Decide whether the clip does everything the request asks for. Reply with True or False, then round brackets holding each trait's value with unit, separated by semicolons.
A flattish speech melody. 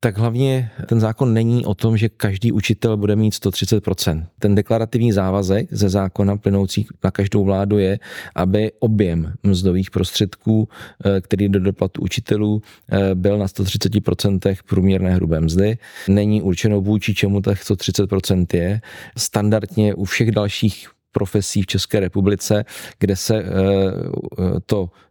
True (2.0 semitones)